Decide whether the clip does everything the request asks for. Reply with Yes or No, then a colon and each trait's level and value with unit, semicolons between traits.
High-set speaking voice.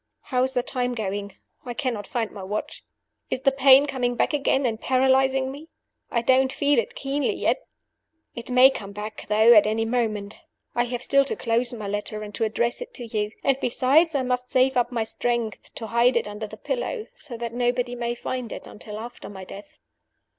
Yes: high, 245 Hz